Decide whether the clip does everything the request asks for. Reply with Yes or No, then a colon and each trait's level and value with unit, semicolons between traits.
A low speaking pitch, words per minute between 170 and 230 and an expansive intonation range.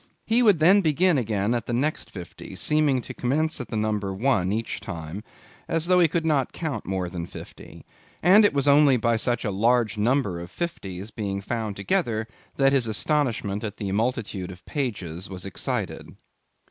Yes: low, 115 Hz; average, 180 wpm; wide, 6.8 semitones